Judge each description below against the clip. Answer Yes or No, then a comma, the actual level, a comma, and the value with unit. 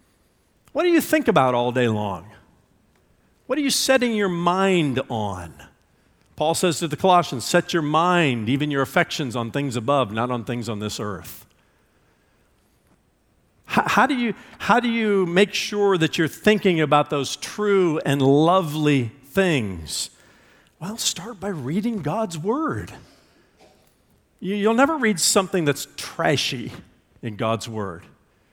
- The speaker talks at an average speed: Yes, average, 145 wpm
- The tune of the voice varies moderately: No, wide, 8.5 semitones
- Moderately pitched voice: Yes, medium, 160 Hz